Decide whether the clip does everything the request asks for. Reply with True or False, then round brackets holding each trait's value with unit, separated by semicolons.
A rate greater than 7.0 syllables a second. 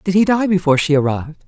True (7.4 syllables/s)